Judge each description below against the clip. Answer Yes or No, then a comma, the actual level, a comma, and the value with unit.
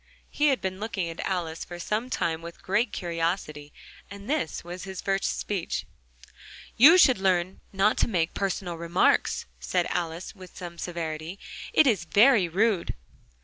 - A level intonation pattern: No, average, 3.4 semitones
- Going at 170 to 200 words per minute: No, average, 150 wpm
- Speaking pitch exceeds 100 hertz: Yes, medium, 185 Hz